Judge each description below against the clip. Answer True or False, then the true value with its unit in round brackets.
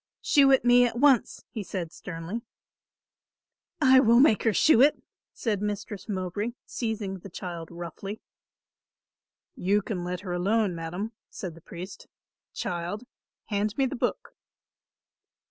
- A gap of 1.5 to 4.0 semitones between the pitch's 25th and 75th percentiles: False (4.6 semitones)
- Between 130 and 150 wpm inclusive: True (135 wpm)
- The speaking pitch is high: True (205 Hz)